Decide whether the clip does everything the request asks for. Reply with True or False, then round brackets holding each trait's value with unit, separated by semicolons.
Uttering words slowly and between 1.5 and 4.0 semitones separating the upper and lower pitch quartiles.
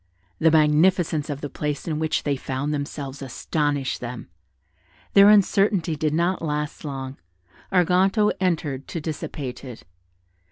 True (130 wpm; 3.4 semitones)